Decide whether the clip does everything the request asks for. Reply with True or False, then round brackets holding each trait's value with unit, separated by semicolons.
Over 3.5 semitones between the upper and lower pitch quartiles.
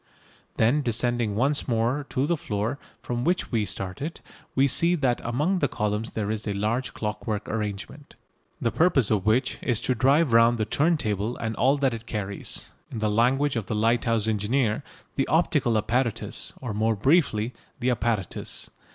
True (4.0 semitones)